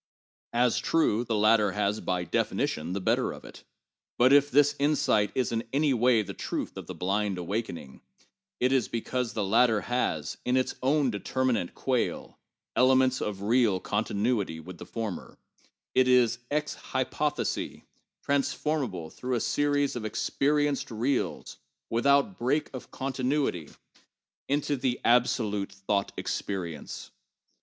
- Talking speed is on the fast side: No, average, 145 wpm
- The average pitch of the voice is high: No, low, 120 Hz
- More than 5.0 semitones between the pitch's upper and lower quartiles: No, average, 4.5 semitones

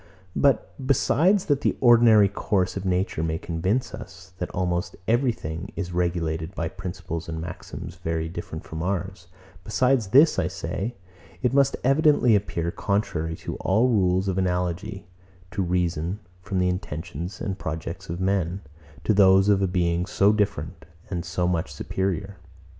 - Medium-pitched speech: No, very low, 95 Hz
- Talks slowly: No, average, 155 wpm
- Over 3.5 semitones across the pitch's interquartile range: No, average, 3.2 semitones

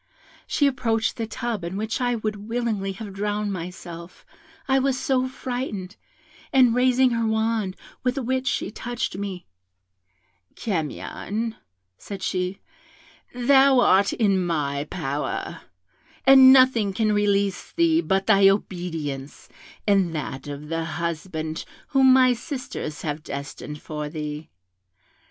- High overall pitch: Yes, high, 205 Hz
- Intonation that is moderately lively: No, wide, 6.3 semitones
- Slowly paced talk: Yes, slow, 125 wpm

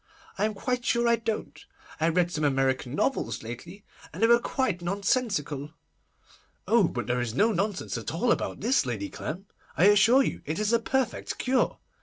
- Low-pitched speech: No, high, 195 Hz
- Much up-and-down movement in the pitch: Yes, wide, 7.9 semitones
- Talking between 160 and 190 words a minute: Yes, average, 185 wpm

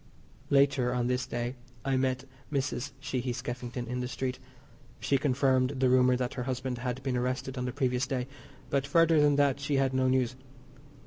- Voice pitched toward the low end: Yes, low, 130 Hz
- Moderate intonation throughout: No, narrow, 1.4 semitones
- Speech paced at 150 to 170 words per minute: No, average, 185 wpm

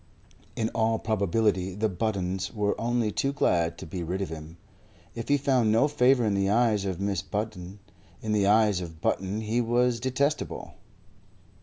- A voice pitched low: Yes, low, 105 Hz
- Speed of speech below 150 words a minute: No, average, 170 wpm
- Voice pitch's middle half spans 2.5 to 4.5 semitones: Yes, average, 3.5 semitones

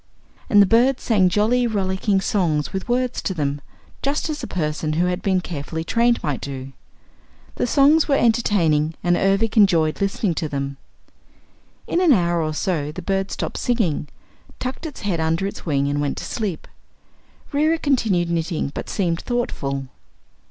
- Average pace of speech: Yes, average, 165 wpm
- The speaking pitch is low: No, medium, 185 Hz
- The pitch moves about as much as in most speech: No, wide, 6.7 semitones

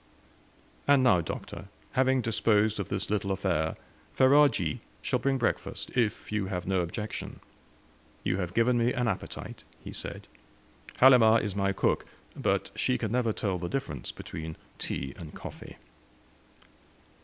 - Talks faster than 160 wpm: No, average, 145 wpm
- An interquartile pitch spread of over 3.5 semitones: Yes, average, 5.0 semitones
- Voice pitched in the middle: No, low, 105 Hz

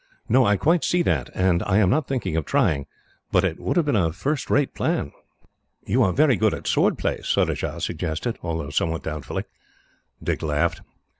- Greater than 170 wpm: Yes, average, 190 wpm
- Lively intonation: Yes, wide, 8.7 semitones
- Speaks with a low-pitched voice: Yes, very low, 95 Hz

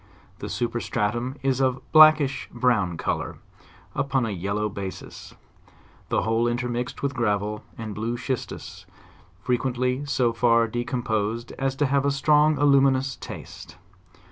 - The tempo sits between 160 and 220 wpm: No, average, 140 wpm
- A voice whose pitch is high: No, low, 120 Hz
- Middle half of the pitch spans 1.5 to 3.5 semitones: Yes, average, 3.2 semitones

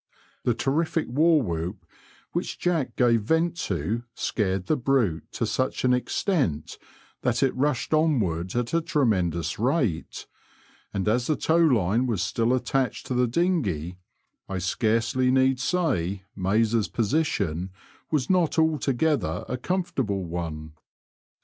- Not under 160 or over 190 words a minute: No, slow, 135 wpm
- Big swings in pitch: Yes, wide, 7.6 semitones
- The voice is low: Yes, low, 120 Hz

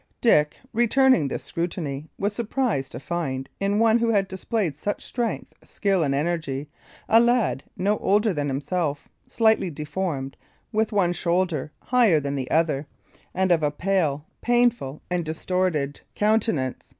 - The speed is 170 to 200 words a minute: No, average, 145 wpm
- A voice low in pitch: No, medium, 175 Hz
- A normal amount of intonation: No, wide, 6.3 semitones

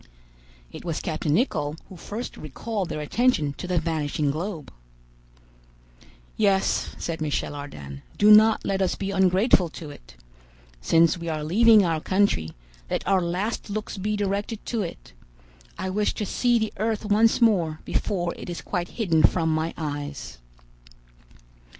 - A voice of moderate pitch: Yes, medium, 180 Hz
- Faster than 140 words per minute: Yes, average, 150 wpm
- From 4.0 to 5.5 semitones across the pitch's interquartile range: Yes, average, 5.0 semitones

